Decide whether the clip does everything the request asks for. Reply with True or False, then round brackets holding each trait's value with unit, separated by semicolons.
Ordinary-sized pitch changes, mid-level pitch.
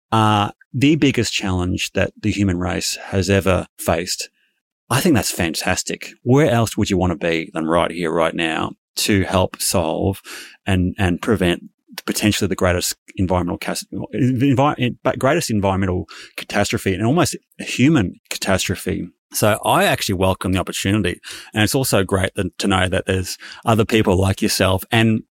False (3.2 semitones; 100 Hz)